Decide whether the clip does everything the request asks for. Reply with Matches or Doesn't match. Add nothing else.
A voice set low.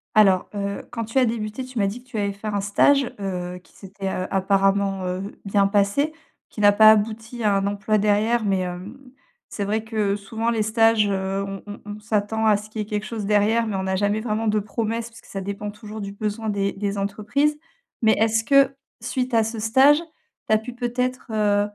Doesn't match